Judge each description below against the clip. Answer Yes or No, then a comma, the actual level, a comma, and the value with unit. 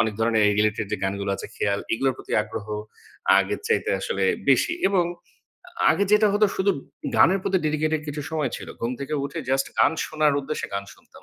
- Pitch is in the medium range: Yes, medium, 150 Hz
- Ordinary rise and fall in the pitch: No, wide, 8.0 semitones